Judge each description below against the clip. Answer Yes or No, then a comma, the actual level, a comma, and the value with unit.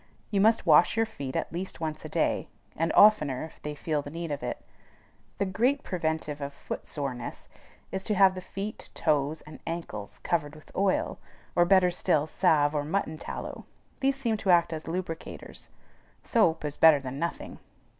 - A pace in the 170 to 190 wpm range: Yes, average, 180 wpm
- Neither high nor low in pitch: Yes, medium, 165 Hz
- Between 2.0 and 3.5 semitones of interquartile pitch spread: No, average, 4.3 semitones